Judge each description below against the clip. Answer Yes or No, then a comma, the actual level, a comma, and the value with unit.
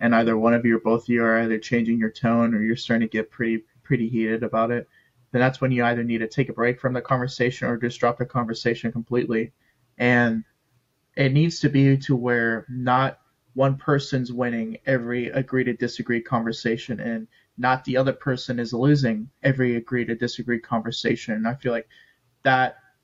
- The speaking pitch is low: Yes, low, 120 Hz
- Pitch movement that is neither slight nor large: No, narrow, 2.0 semitones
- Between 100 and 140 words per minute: No, average, 200 wpm